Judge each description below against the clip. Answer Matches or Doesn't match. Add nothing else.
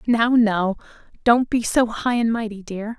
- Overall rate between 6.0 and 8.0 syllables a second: Doesn't match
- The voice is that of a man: Doesn't match